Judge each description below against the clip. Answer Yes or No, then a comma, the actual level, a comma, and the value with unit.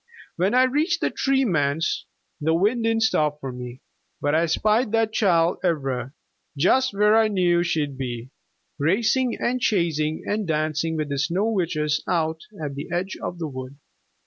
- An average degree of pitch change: No, wide, 6.2 semitones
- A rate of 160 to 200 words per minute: Yes, average, 170 wpm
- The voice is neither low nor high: Yes, medium, 170 Hz